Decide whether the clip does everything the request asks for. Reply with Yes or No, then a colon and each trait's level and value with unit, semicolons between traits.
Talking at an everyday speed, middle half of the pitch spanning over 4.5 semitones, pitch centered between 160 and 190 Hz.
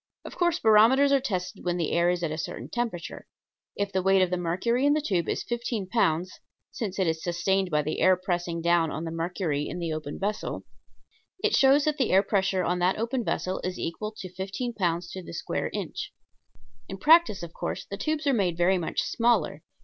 No: fast, 210 wpm; average, 4.9 semitones; medium, 185 Hz